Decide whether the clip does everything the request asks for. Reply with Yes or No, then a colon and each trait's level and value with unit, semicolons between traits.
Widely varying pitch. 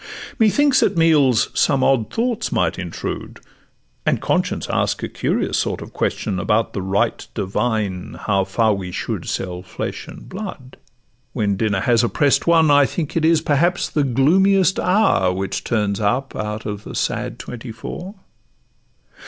Yes: wide, 8.3 semitones